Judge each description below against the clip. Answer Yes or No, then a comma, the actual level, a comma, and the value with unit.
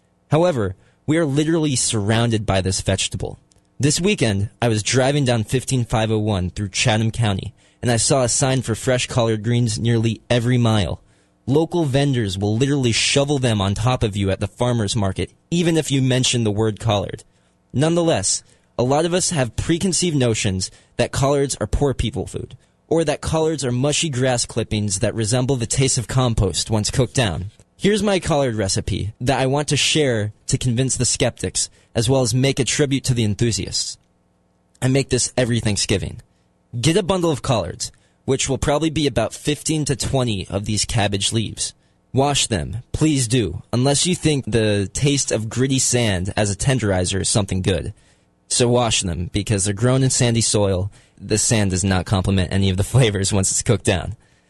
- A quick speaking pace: No, average, 180 wpm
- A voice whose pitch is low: Yes, low, 115 Hz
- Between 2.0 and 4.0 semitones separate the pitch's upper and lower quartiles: No, average, 4.6 semitones